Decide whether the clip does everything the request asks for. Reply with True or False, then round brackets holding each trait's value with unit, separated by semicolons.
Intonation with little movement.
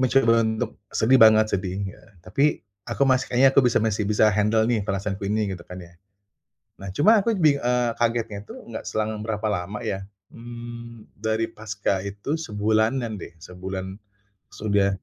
False (3.0 semitones)